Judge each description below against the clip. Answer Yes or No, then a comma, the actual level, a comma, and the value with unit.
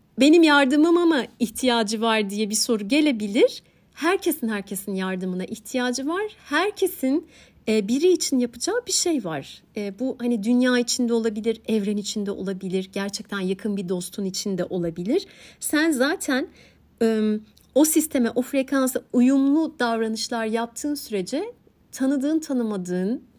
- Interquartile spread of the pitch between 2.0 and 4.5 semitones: No, wide, 5.4 semitones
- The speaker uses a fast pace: No, average, 120 wpm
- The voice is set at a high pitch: Yes, high, 240 Hz